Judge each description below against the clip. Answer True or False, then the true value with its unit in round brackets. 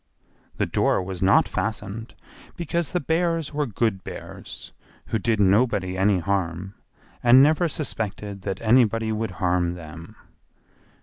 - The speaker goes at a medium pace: False (130 wpm)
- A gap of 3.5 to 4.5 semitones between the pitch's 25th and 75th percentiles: False (4.9 semitones)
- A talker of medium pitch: False (105 Hz)